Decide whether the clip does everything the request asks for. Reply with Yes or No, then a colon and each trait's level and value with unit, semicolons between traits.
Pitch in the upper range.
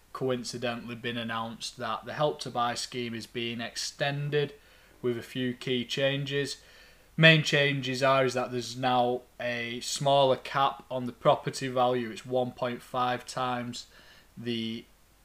No: low, 125 Hz